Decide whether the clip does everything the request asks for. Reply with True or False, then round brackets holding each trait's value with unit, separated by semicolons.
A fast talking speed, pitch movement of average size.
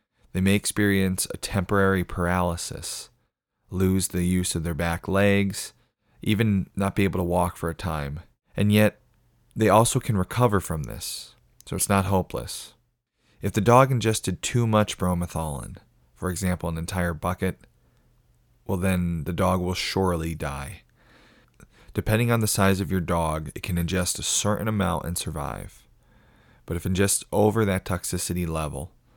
False (155 wpm; 3.2 semitones)